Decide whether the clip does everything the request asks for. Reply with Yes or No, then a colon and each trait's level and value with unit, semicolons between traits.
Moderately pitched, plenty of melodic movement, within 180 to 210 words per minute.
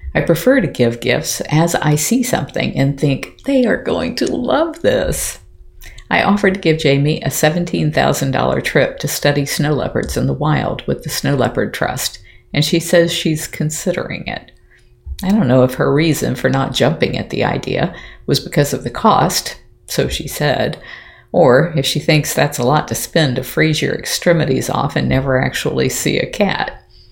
No: medium, 155 Hz; average, 4.4 semitones; average, 185 wpm